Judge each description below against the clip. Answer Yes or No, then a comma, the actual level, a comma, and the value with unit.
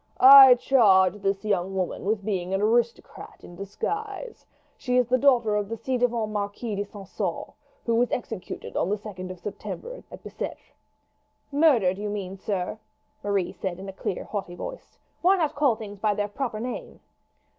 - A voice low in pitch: No, high, 210 Hz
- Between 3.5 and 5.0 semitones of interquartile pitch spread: Yes, average, 4.2 semitones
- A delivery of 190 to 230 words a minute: No, average, 175 wpm